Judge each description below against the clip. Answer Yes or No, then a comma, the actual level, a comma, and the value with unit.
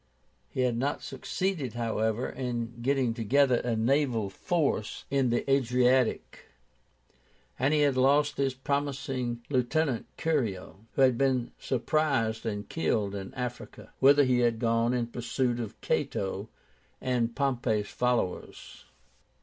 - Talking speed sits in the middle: No, slow, 125 wpm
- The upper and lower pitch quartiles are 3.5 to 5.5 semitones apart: No, average, 2.9 semitones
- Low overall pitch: Yes, low, 125 Hz